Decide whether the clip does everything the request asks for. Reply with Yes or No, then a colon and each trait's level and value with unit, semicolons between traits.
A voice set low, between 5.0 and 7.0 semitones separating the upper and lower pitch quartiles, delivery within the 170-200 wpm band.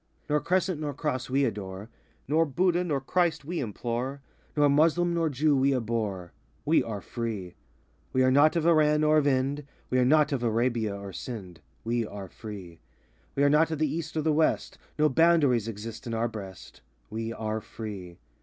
Yes: low, 130 Hz; wide, 5.6 semitones; average, 185 wpm